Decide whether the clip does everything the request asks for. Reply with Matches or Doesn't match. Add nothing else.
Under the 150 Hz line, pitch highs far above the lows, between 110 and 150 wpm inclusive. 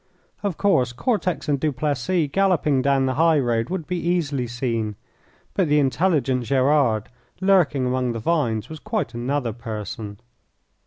Matches